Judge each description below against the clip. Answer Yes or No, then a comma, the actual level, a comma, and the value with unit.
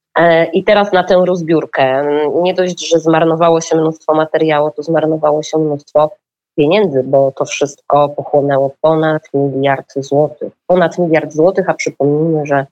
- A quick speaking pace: No, average, 140 wpm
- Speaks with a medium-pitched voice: Yes, medium, 155 Hz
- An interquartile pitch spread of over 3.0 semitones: No, narrow, 2.4 semitones